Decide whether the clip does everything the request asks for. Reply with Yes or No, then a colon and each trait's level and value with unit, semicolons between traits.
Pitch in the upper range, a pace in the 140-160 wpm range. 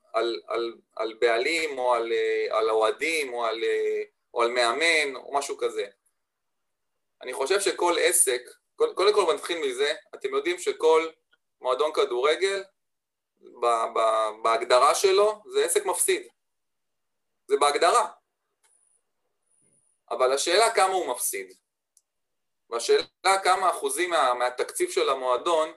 No: very high, 395 Hz; average, 115 wpm